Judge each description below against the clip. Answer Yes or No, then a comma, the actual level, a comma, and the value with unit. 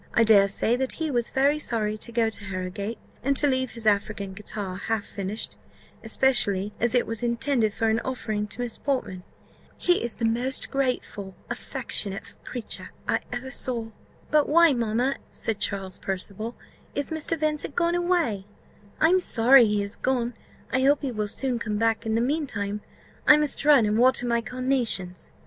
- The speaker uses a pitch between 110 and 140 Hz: No, high, 235 Hz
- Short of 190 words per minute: Yes, average, 180 wpm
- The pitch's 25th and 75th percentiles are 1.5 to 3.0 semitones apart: No, average, 4.1 semitones